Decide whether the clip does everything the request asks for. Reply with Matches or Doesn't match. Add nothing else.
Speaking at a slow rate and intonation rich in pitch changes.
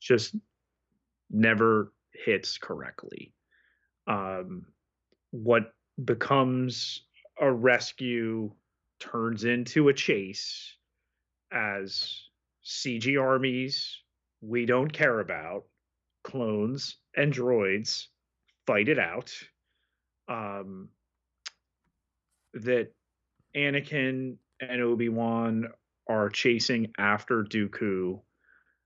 Doesn't match